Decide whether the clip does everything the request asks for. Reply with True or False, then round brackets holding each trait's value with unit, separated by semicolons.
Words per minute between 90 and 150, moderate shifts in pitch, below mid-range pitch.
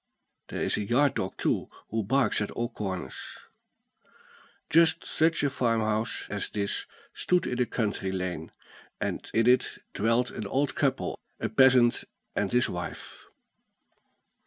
True (140 wpm; 4.0 semitones; 115 Hz)